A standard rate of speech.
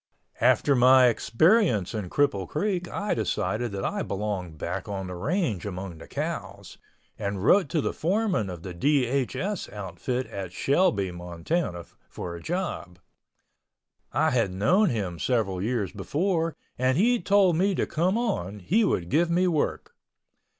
Yes: average, 150 wpm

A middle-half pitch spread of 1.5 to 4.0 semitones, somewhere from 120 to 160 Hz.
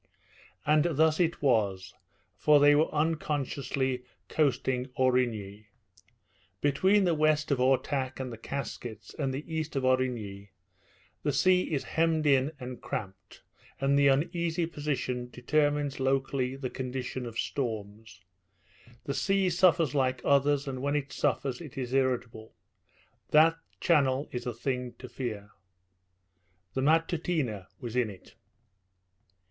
Yes: average, 3.3 semitones; low, 135 Hz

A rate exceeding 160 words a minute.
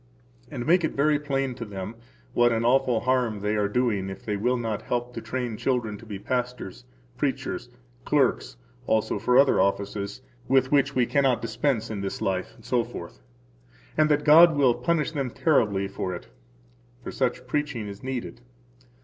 Yes: average, 170 wpm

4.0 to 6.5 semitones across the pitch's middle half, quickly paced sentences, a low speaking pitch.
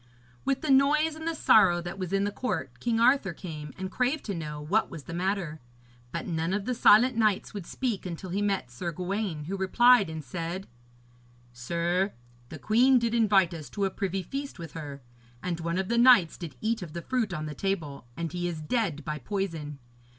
No: average, 5.2 semitones; fast, 210 wpm; high, 190 Hz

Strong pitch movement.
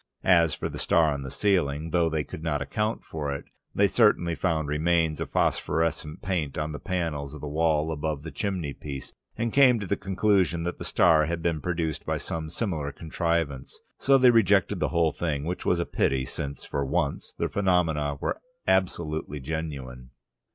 No: average, 3.3 semitones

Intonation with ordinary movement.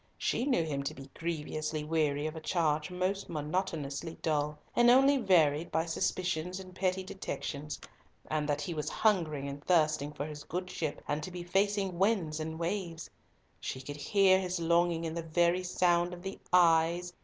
Yes: average, 3.2 semitones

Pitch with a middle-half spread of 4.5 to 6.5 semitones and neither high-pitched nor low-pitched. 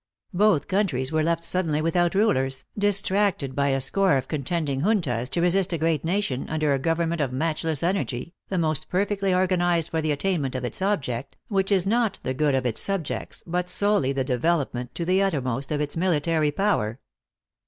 Yes: wide, 5.4 semitones; medium, 165 Hz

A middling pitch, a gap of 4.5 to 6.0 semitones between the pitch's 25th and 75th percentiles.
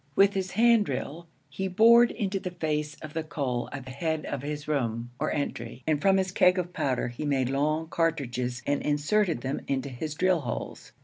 Yes: medium, 150 Hz; average, 5.0 semitones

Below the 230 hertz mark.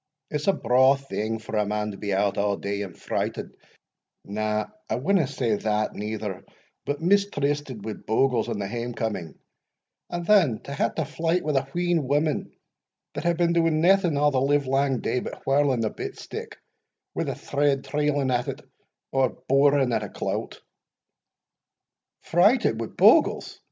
Yes: low, 135 Hz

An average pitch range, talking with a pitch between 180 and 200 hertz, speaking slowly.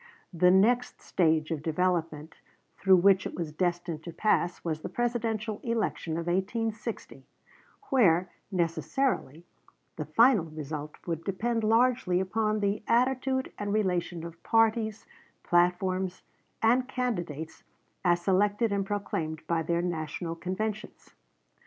Yes: average, 4.7 semitones; medium, 185 Hz; slow, 120 wpm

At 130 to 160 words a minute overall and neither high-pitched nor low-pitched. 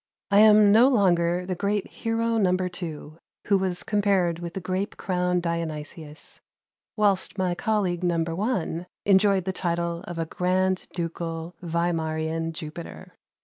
Yes: average, 140 wpm; medium, 180 Hz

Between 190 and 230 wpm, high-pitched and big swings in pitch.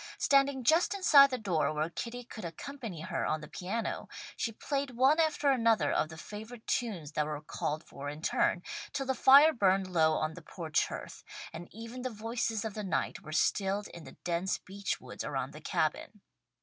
Yes: average, 195 wpm; high, 210 Hz; wide, 7.3 semitones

